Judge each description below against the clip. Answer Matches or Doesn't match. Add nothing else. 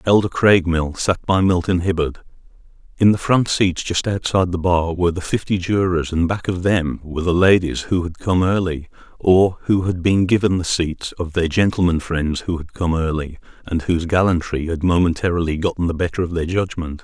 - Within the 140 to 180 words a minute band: Doesn't match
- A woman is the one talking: Doesn't match